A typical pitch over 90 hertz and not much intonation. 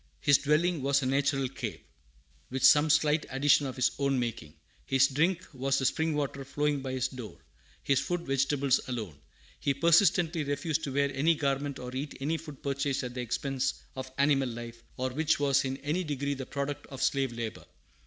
Yes: medium, 140 Hz; narrow, 2.0 semitones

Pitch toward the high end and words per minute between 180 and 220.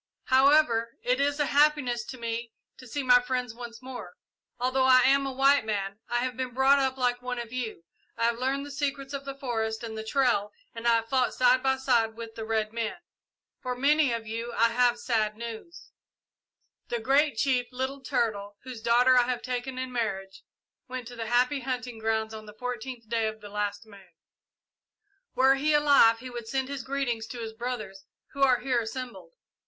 Yes: high, 245 Hz; average, 200 wpm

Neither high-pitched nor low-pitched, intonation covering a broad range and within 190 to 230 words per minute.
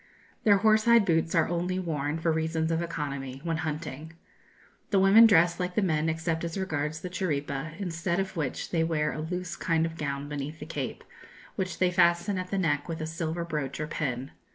No: medium, 165 Hz; average, 2.9 semitones; average, 200 wpm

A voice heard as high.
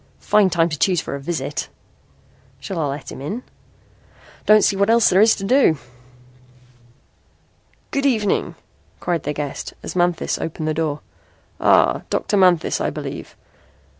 No: medium, 175 Hz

